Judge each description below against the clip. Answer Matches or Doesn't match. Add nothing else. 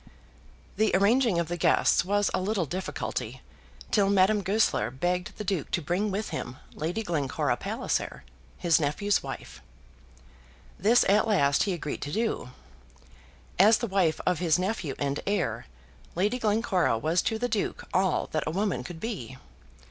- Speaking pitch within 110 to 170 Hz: Doesn't match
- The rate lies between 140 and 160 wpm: Matches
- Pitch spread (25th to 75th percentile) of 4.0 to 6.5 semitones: Matches